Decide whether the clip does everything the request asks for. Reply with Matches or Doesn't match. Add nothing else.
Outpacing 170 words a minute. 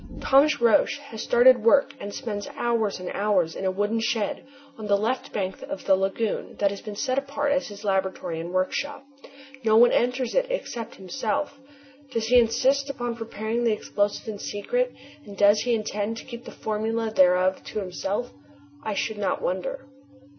Matches